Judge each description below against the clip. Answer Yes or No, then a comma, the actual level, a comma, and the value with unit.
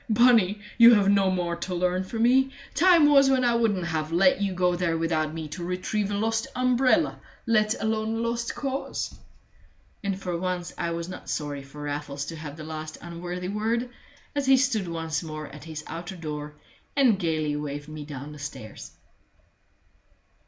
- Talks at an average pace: Yes, average, 180 wpm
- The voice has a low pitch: No, medium, 180 Hz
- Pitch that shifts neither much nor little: No, wide, 6.2 semitones